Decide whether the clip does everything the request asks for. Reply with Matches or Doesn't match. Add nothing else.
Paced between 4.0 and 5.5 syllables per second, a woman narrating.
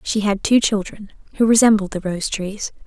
Matches